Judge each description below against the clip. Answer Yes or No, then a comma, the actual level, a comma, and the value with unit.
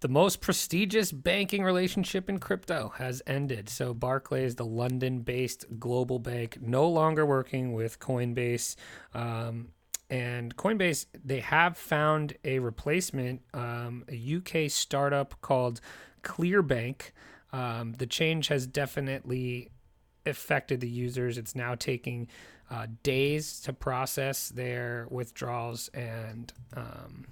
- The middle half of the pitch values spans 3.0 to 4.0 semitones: Yes, average, 3.5 semitones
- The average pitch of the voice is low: Yes, low, 130 Hz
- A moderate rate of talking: No, slow, 120 wpm